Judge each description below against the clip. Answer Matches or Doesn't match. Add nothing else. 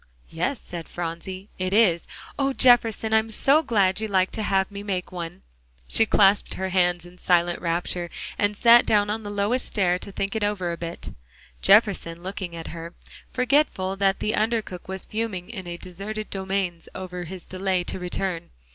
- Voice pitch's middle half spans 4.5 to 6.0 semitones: Doesn't match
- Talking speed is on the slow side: Doesn't match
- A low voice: Doesn't match